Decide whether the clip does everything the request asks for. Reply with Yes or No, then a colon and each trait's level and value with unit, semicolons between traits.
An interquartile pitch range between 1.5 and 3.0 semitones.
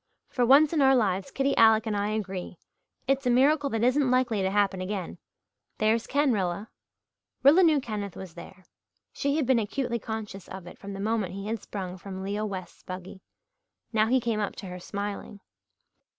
No: average, 4.6 semitones